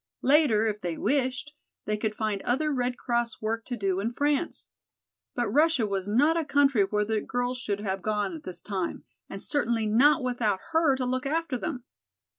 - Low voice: No, high, 245 Hz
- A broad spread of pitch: No, average, 5.0 semitones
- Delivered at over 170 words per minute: Yes, average, 190 wpm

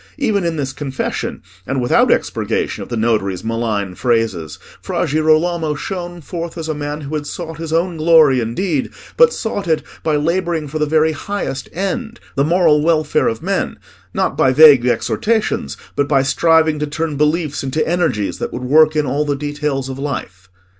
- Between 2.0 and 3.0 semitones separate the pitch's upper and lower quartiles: No, average, 3.9 semitones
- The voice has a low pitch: No, medium, 150 Hz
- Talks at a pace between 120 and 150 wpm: No, average, 175 wpm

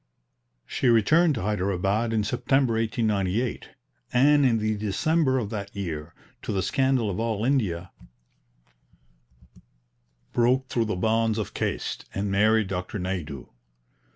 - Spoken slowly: Yes, slow, 125 wpm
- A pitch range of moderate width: Yes, average, 3.9 semitones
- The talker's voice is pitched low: Yes, low, 110 Hz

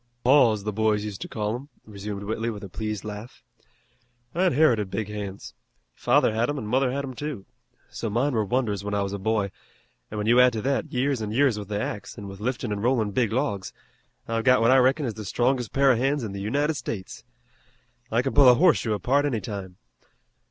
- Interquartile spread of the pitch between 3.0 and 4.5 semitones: Yes, average, 3.9 semitones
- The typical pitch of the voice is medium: No, low, 115 Hz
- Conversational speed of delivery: No, fast, 220 wpm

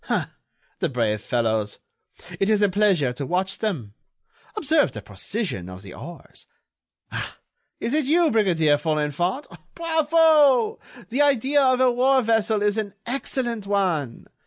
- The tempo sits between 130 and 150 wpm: Yes, average, 140 wpm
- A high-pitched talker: Yes, high, 205 Hz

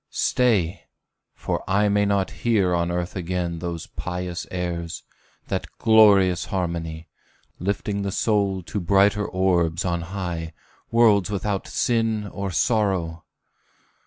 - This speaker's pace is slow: Yes, slow, 120 wpm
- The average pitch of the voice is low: Yes, very low, 95 Hz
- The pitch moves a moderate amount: Yes, average, 3.0 semitones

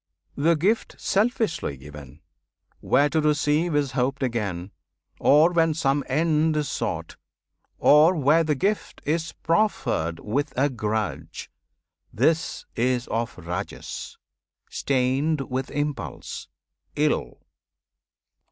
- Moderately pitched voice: Yes, medium, 145 Hz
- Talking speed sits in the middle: No, slow, 105 wpm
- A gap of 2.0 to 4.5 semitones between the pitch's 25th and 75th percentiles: No, average, 5.0 semitones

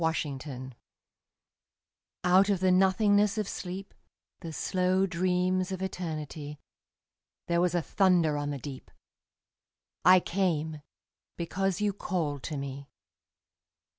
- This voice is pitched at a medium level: Yes, medium, 180 Hz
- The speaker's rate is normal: No, slow, 115 wpm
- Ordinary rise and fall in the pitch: Yes, average, 3.8 semitones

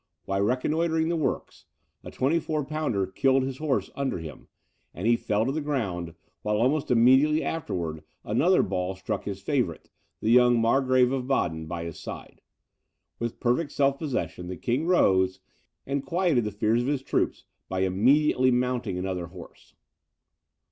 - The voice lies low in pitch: Yes, low, 125 Hz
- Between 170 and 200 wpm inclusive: No, average, 155 wpm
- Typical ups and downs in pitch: No, wide, 6.7 semitones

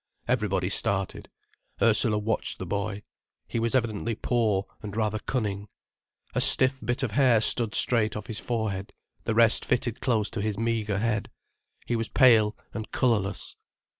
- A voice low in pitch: Yes, low, 110 Hz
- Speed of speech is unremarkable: Yes, average, 155 wpm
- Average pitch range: No, narrow, 2.1 semitones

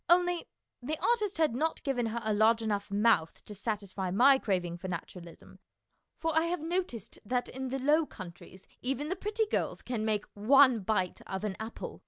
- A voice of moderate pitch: No, high, 230 Hz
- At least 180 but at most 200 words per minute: Yes, average, 185 wpm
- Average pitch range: No, wide, 7.1 semitones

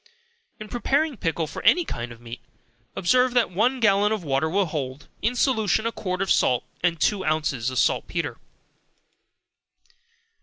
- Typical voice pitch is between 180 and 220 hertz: Yes, high, 190 Hz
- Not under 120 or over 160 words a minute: Yes, average, 155 wpm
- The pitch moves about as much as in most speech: No, wide, 7.3 semitones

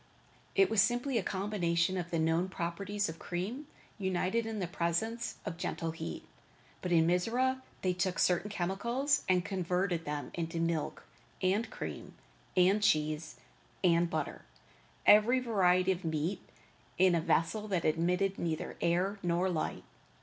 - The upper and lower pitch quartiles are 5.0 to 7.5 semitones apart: No, average, 3.5 semitones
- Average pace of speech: Yes, average, 150 wpm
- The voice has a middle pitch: Yes, medium, 180 Hz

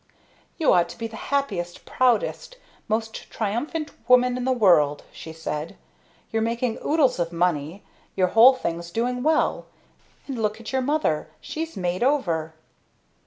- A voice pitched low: No, high, 225 Hz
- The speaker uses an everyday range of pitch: No, wide, 6.8 semitones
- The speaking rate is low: No, average, 150 wpm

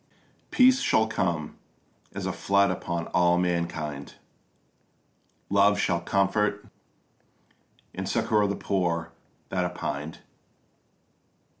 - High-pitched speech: No, very low, 90 Hz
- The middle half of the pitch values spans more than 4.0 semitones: No, average, 3.1 semitones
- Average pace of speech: No, slow, 100 wpm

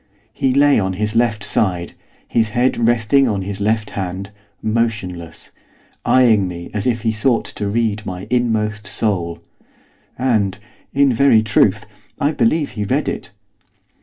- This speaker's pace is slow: No, average, 145 wpm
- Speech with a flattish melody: No, average, 3.4 semitones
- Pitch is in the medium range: No, low, 110 Hz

